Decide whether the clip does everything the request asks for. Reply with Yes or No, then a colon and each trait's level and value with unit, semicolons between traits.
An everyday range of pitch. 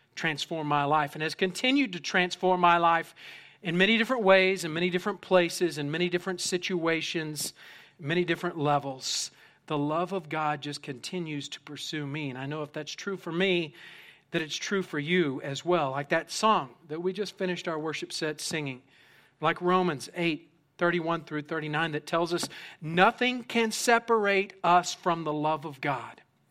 Yes: average, 3.1 semitones